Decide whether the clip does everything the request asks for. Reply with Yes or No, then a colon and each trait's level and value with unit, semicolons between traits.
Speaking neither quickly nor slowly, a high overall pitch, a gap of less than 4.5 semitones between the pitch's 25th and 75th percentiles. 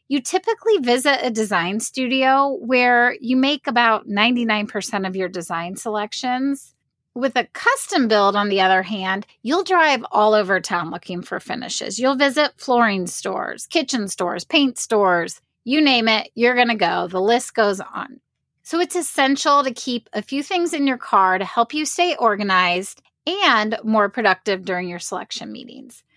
No: average, 165 wpm; high, 235 Hz; wide, 5.6 semitones